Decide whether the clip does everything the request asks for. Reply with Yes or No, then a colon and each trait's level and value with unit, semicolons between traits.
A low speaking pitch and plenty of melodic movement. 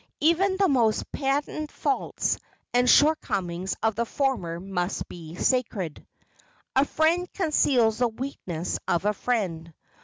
No: high, 235 Hz; wide, 8.1 semitones